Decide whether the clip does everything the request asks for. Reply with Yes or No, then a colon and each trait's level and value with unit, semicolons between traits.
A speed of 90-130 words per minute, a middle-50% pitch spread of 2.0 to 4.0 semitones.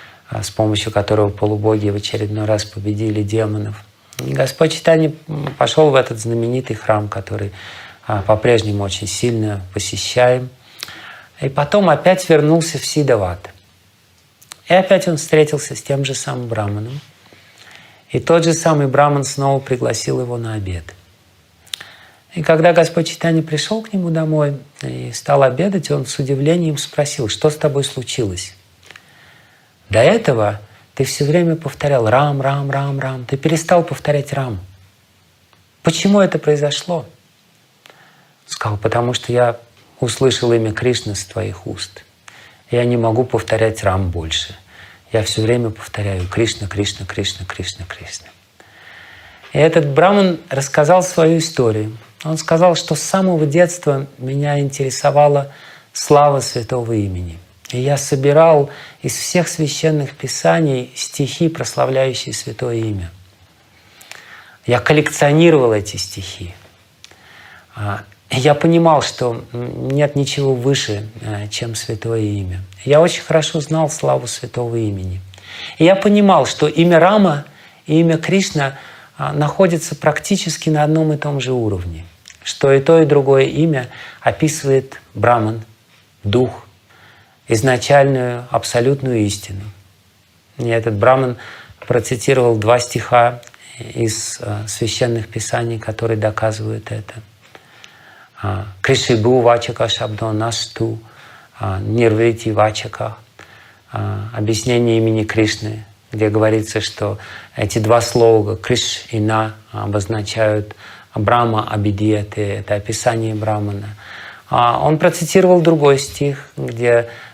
No: average, 115 wpm; average, 5.3 semitones